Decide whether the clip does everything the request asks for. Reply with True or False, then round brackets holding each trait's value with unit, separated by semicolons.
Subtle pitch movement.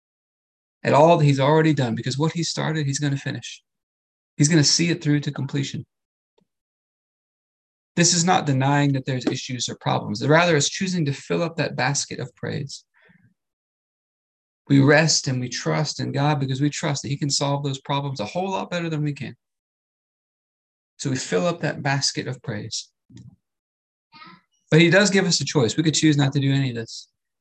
False (3.2 semitones)